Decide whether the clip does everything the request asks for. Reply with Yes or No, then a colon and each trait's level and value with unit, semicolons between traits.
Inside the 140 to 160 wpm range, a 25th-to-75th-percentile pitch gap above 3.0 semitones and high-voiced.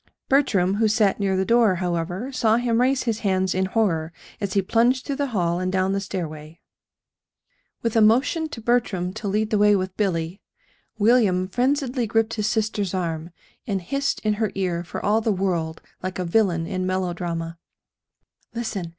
No: average, 175 wpm; average, 3.8 semitones; high, 200 Hz